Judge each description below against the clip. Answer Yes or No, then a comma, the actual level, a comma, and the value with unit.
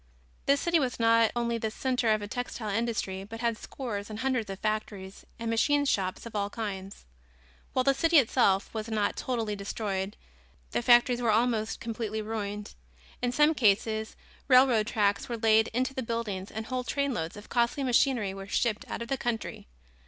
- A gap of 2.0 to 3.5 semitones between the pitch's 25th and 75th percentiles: Yes, average, 3.0 semitones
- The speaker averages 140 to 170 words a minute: No, average, 180 wpm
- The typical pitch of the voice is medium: No, high, 225 Hz